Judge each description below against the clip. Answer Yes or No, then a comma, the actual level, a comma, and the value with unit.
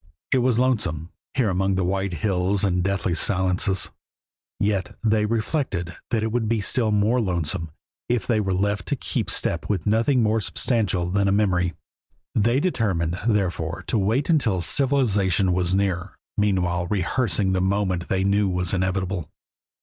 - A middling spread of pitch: Yes, average, 3.3 semitones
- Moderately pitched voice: No, low, 100 Hz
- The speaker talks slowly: No, average, 160 wpm